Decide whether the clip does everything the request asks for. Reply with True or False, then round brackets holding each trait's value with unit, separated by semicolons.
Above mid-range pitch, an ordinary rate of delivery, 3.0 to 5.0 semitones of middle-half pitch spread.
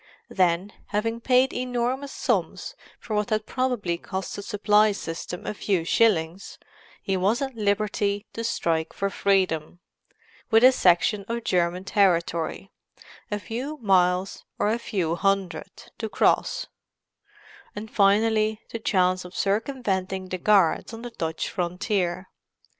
False (200 Hz; 125 wpm; 3.7 semitones)